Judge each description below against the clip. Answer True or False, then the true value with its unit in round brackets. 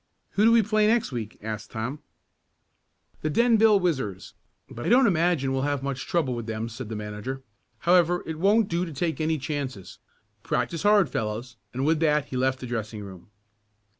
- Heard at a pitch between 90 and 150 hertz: True (140 Hz)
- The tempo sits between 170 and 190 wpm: True (185 wpm)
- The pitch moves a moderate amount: False (7.1 semitones)